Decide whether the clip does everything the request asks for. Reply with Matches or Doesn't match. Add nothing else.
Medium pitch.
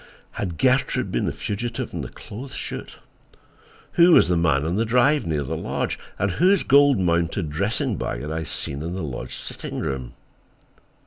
Doesn't match